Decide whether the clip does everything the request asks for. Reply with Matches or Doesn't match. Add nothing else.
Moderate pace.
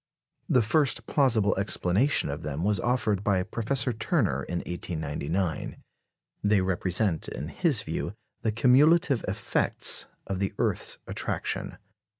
Doesn't match